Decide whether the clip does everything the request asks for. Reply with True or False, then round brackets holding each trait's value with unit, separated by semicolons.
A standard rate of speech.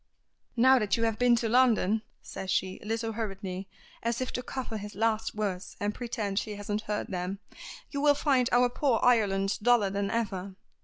True (190 wpm)